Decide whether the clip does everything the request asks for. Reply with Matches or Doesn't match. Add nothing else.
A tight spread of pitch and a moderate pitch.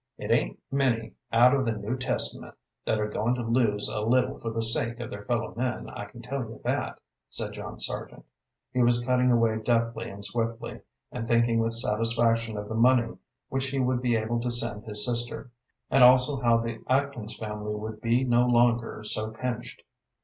Doesn't match